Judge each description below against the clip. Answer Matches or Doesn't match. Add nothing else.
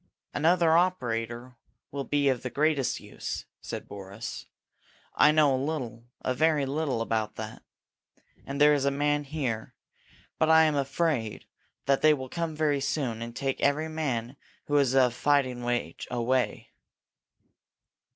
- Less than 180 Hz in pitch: Matches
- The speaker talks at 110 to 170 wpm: Matches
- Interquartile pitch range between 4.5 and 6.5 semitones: Doesn't match